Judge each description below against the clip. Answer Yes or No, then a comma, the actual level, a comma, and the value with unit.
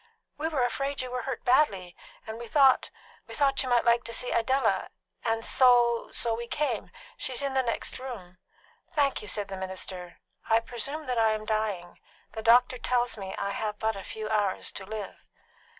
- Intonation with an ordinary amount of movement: Yes, average, 3.4 semitones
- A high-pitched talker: Yes, high, 230 Hz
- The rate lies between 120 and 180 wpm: No, average, 200 wpm